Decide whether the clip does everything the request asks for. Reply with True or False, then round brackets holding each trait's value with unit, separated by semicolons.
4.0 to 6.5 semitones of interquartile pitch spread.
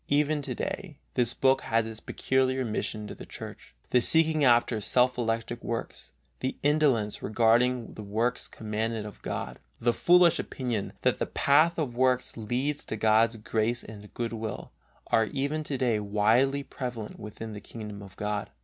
False (3.5 semitones)